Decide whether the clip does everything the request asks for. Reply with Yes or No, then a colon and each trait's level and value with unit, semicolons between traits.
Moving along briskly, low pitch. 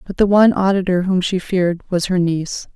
No: fast, 220 wpm; medium, 185 Hz